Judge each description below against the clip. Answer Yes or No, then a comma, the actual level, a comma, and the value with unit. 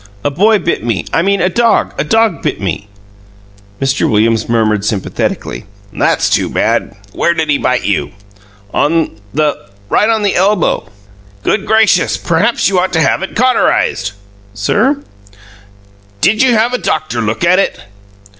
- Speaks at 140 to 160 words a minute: Yes, average, 155 wpm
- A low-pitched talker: No, medium, 165 Hz